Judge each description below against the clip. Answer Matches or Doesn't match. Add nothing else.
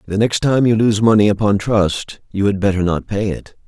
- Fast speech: Matches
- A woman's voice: Doesn't match